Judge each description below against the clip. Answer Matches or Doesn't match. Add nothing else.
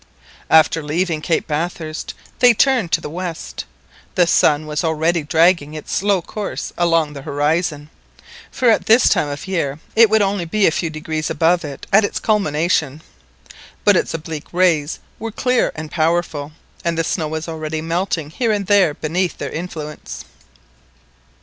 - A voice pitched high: Doesn't match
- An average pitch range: Matches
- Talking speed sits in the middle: Matches